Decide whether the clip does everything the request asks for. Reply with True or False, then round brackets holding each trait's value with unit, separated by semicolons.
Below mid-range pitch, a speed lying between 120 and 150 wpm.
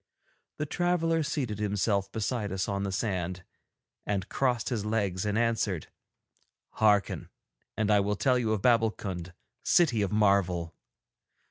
True (105 Hz; 135 wpm)